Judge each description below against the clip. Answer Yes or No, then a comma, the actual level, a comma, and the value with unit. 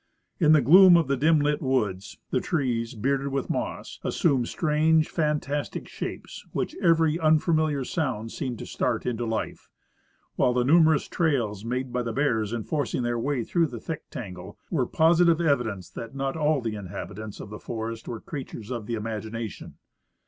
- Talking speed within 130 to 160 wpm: No, average, 185 wpm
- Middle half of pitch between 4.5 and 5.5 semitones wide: Yes, average, 5.2 semitones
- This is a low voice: Yes, low, 130 Hz